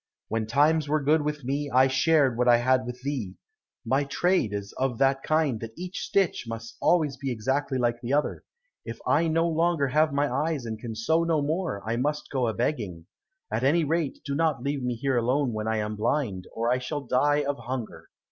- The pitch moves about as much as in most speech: Yes, average, 4.1 semitones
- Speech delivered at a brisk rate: Yes, fast, 215 wpm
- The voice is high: No, low, 135 Hz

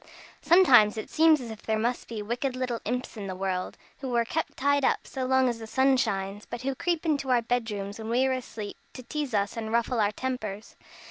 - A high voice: Yes, high, 240 Hz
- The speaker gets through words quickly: Yes, fast, 230 wpm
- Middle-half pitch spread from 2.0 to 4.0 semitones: Yes, average, 3.3 semitones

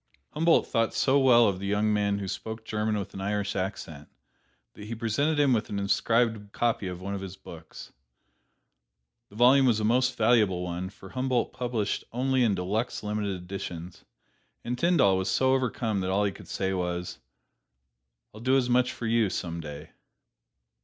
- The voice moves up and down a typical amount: Yes, average, 4.1 semitones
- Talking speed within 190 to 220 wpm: No, average, 180 wpm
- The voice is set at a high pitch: No, low, 105 Hz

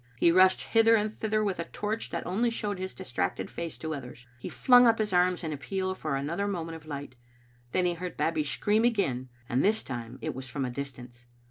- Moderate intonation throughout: No, wide, 7.1 semitones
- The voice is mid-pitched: Yes, medium, 175 Hz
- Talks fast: Yes, fast, 225 wpm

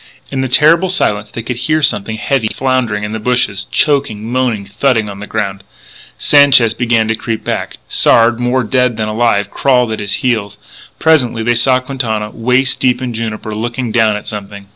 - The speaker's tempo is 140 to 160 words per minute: No, average, 185 wpm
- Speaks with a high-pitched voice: No, low, 115 Hz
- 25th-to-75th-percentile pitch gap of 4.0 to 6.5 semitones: No, average, 3.1 semitones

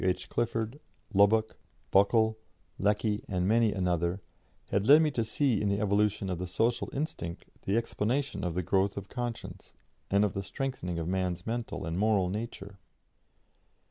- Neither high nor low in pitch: No, low, 105 Hz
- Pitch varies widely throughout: No, average, 3.4 semitones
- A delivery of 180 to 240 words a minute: No, average, 160 wpm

